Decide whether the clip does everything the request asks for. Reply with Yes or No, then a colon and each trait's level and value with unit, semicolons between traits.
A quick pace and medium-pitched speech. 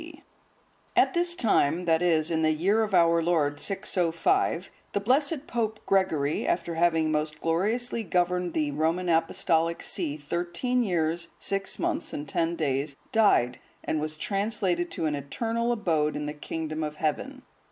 No: average, 155 wpm; medium, 170 Hz